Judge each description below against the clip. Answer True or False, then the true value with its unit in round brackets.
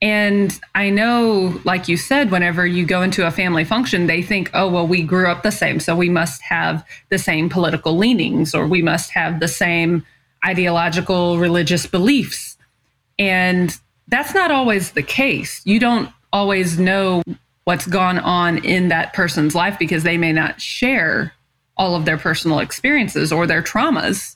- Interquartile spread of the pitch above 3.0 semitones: False (2.7 semitones)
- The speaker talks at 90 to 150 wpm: False (170 wpm)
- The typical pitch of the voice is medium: True (180 Hz)